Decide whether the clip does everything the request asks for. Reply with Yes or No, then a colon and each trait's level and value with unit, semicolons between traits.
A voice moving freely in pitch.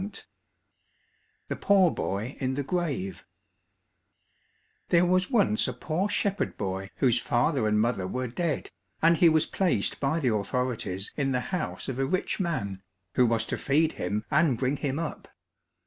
Yes: wide, 6.8 semitones